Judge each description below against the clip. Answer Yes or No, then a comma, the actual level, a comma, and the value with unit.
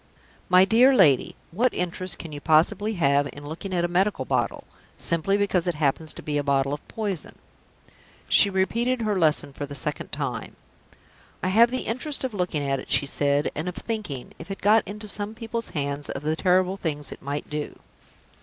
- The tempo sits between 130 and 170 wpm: No, average, 195 wpm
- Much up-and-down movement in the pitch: Yes, wide, 6.0 semitones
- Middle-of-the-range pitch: Yes, medium, 180 Hz